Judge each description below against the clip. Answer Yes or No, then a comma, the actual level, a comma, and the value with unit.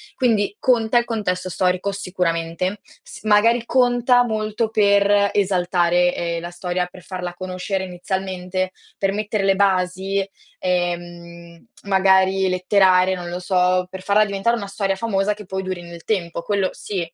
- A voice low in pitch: No, high, 190 Hz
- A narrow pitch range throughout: Yes, narrow, 2.2 semitones